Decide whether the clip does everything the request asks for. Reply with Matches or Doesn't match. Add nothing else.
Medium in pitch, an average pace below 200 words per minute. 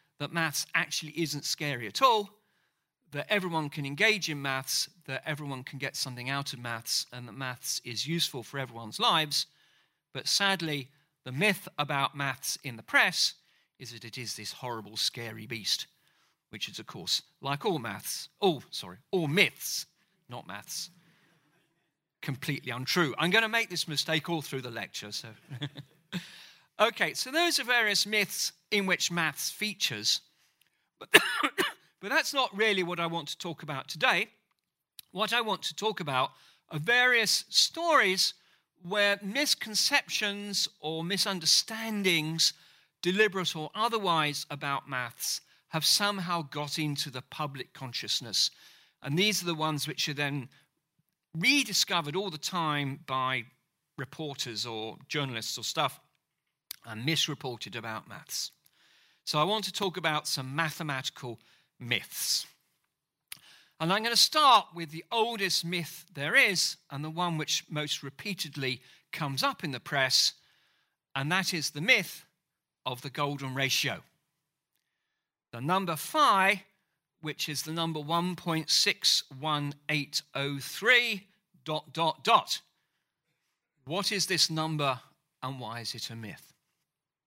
Matches